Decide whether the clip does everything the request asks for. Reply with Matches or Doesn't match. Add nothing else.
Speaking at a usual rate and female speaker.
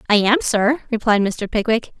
Matches